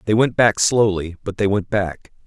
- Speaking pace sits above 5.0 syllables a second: No, 4.7 syllables/s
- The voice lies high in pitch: No, low, 100 Hz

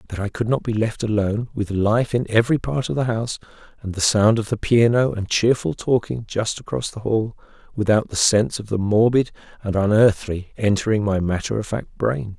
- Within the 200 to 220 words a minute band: Yes, fast, 205 wpm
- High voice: No, low, 110 Hz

